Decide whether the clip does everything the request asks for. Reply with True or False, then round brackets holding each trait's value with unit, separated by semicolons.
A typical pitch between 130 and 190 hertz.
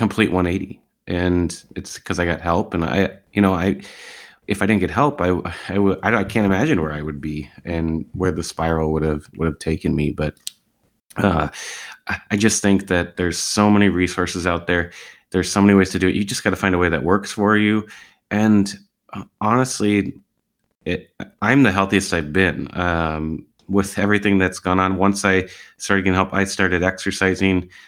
False (95 Hz)